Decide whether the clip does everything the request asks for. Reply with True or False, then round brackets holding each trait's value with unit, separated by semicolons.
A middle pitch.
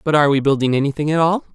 True (150 Hz)